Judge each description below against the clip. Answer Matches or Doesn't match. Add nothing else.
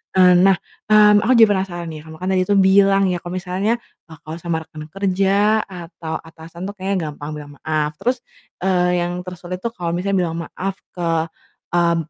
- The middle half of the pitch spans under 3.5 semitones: Matches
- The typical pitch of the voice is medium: Matches